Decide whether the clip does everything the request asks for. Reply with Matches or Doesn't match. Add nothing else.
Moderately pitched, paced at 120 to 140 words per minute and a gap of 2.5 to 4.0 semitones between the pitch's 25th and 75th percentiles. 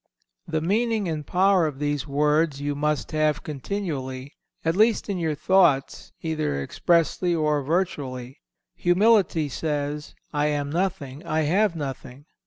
Matches